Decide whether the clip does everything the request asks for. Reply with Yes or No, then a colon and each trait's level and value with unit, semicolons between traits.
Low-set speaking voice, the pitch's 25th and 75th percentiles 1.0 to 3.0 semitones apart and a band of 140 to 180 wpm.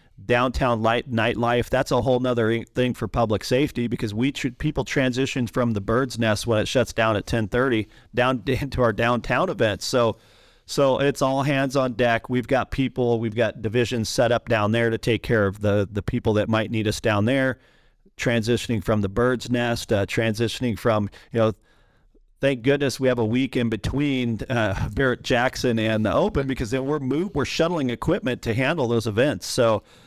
No: low, 120 Hz; narrow, 2.5 semitones; average, 195 wpm